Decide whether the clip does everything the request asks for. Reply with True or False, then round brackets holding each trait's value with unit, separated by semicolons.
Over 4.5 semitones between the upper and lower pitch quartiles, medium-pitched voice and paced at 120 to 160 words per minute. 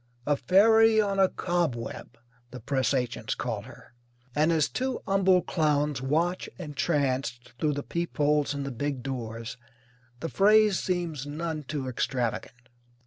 True (5.2 semitones; 150 Hz; 140 wpm)